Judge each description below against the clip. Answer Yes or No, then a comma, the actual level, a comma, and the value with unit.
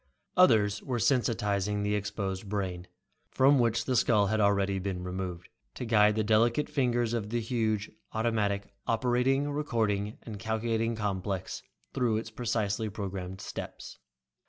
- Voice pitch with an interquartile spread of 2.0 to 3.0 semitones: Yes, average, 2.7 semitones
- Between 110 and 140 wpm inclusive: Yes, slow, 135 wpm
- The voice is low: Yes, low, 110 Hz